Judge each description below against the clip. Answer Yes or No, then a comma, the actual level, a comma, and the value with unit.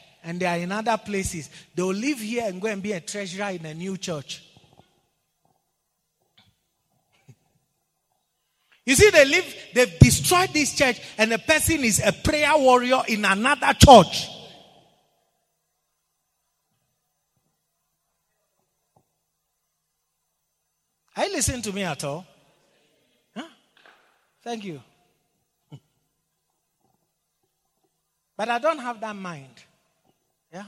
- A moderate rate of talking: No, slow, 105 wpm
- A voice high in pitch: Yes, high, 195 Hz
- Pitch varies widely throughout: Yes, wide, 6.8 semitones